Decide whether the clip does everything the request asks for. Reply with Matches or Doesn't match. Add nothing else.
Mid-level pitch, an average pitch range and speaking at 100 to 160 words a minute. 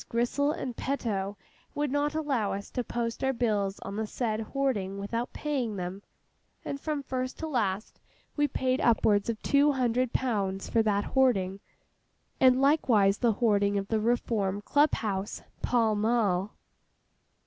Doesn't match